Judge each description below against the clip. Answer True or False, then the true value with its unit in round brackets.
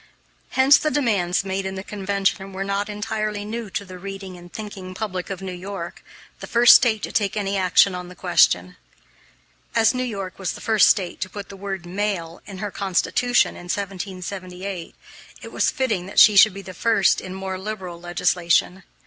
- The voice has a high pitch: True (195 Hz)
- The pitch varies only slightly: True (2.2 semitones)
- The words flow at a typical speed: True (185 wpm)